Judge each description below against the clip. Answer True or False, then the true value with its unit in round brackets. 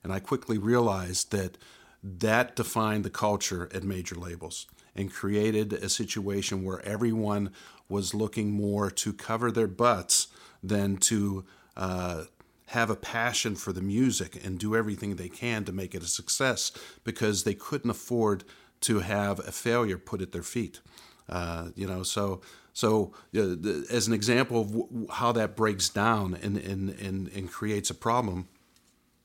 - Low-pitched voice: True (100 Hz)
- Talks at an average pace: True (160 wpm)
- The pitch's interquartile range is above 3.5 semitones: False (2.9 semitones)